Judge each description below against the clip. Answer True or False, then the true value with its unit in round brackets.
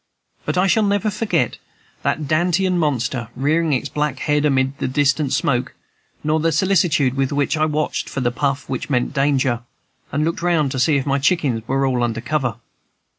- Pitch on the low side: False (145 Hz)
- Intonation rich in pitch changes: False (3.2 semitones)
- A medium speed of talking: True (185 wpm)